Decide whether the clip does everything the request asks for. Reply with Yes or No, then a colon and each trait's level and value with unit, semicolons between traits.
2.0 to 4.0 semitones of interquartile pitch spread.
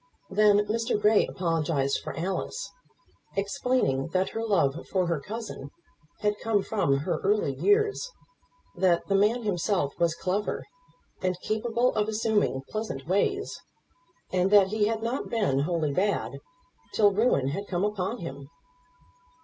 No: average, 4.4 semitones